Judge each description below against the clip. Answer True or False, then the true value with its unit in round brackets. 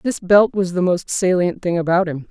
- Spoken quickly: True (235 wpm)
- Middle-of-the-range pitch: True (180 Hz)